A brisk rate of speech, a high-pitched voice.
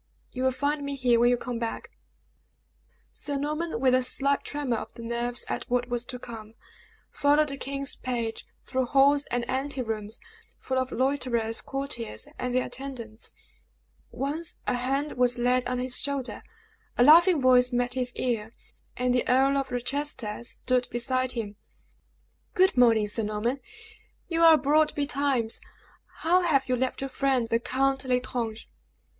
No: average, 160 wpm; very high, 255 Hz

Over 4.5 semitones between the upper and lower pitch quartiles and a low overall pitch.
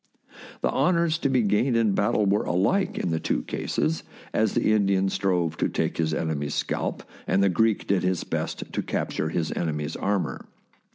Yes: average, 4.9 semitones; very low, 95 Hz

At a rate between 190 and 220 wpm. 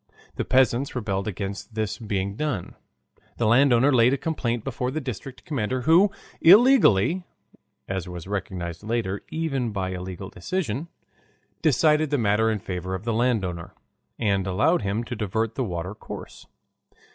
No: average, 155 wpm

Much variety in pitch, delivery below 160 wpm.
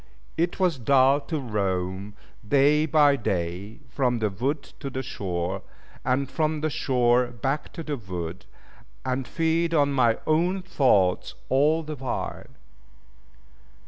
Yes: wide, 6.4 semitones; slow, 135 wpm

